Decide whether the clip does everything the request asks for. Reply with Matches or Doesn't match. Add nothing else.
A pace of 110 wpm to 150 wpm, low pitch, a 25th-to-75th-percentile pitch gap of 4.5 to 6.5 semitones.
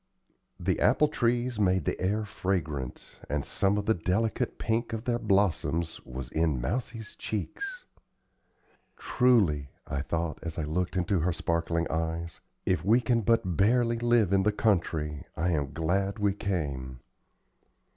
Matches